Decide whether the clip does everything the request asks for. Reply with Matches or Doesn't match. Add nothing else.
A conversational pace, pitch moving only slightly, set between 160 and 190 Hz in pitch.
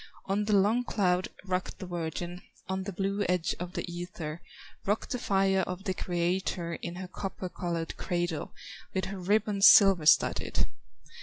Matches